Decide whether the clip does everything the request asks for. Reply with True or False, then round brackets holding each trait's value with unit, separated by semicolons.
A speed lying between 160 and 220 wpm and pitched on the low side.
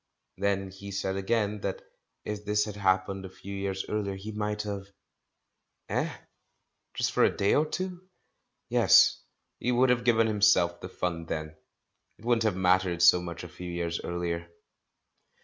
True (170 wpm; 100 Hz)